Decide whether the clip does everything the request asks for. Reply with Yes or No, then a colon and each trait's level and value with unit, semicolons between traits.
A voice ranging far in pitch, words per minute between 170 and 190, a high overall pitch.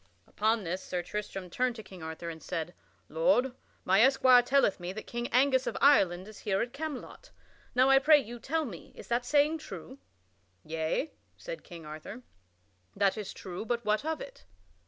Yes: wide, 6.5 semitones; average, 180 wpm; high, 235 Hz